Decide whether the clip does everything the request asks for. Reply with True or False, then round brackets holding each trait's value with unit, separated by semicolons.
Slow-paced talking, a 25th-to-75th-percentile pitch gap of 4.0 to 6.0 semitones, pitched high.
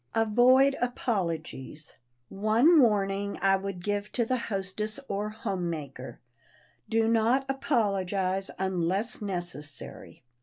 False (105 wpm; 3.5 semitones; 200 Hz)